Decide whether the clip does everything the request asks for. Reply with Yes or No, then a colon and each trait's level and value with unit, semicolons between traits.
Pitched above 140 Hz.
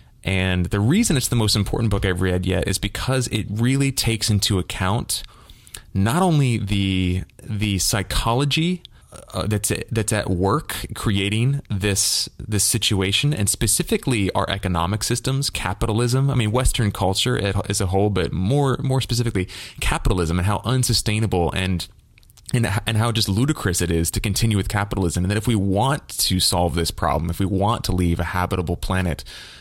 No: low, 105 Hz